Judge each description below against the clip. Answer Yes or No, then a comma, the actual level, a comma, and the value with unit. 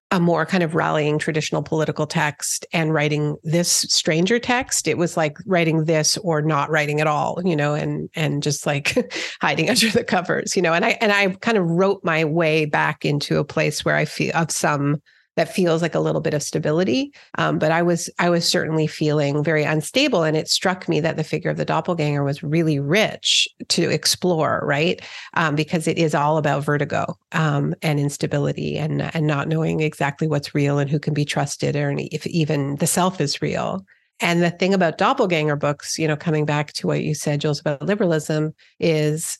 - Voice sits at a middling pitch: Yes, medium, 155 Hz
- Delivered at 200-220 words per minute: Yes, fast, 205 wpm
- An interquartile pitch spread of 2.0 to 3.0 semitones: Yes, narrow, 2.5 semitones